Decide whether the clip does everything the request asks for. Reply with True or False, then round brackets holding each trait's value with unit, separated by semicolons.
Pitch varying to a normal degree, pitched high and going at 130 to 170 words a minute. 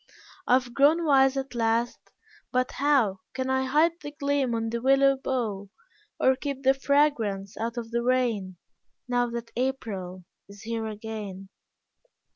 True (3.4 semitones; 245 Hz; 150 wpm)